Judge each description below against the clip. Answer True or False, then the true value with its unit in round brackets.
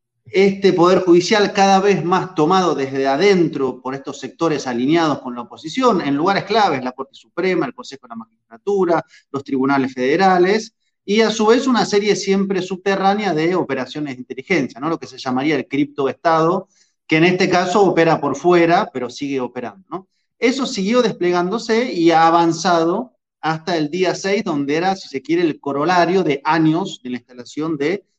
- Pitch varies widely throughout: True (5.8 semitones)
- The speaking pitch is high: False (170 Hz)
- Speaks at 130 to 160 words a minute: False (175 wpm)